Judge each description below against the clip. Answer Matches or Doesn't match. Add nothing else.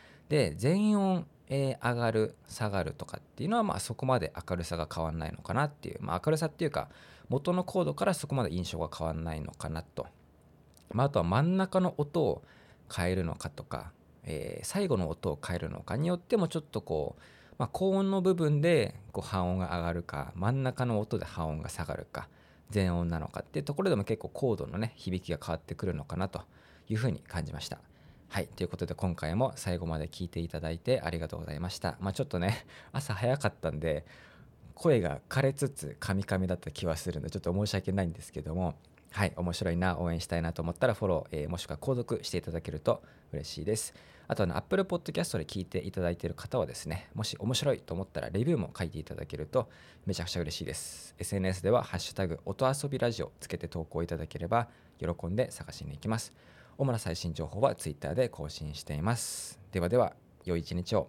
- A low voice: Matches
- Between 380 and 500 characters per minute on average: Matches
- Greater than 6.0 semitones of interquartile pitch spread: Matches